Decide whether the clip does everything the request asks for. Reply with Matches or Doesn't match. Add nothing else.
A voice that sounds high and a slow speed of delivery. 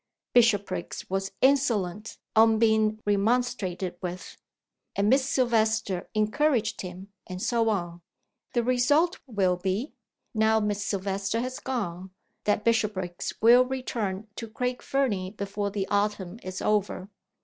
Matches